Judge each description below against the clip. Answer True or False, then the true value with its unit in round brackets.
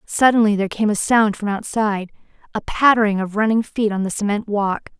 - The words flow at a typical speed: True (180 wpm)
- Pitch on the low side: False (210 Hz)